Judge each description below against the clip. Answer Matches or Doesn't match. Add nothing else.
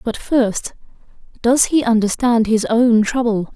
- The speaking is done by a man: Doesn't match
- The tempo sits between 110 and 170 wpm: Matches